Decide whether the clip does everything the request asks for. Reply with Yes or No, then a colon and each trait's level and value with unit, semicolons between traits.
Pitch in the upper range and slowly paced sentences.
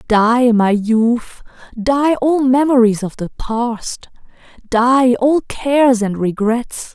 Yes: high, 240 Hz; slow, 120 wpm